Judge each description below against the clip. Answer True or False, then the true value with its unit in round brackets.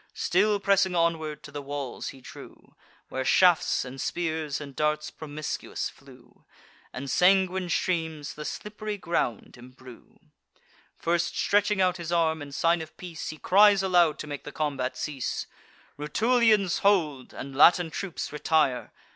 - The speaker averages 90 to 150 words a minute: True (145 wpm)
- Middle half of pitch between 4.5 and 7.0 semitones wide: False (4.1 semitones)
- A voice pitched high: False (160 Hz)